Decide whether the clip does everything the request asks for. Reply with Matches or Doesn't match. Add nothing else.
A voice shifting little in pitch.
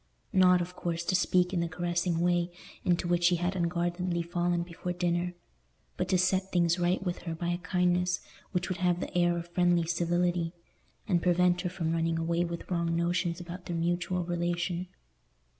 Matches